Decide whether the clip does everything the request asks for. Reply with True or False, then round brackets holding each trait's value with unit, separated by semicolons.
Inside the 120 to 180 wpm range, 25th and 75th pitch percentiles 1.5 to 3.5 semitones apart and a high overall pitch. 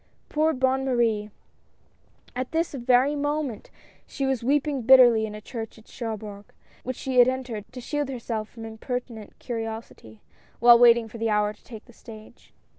True (170 wpm; 3.0 semitones; 240 Hz)